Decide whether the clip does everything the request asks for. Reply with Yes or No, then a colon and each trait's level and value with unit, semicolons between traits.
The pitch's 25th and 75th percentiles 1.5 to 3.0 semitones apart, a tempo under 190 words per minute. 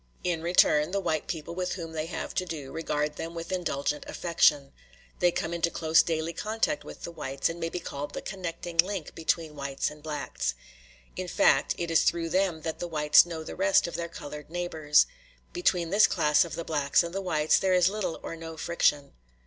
No: narrow, 2.5 semitones; fast, 205 wpm